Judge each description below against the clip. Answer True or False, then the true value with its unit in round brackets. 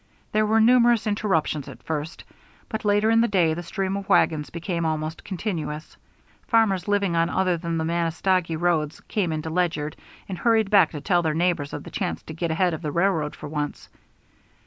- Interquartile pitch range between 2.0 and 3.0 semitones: False (3.9 semitones)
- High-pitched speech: False (175 Hz)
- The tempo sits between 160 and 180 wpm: False (190 wpm)